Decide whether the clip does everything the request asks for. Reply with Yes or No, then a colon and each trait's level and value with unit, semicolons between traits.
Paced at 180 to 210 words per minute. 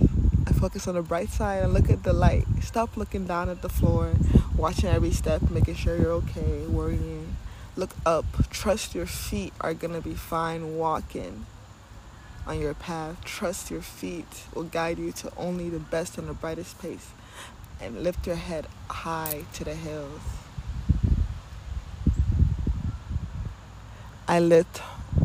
No: average, 150 wpm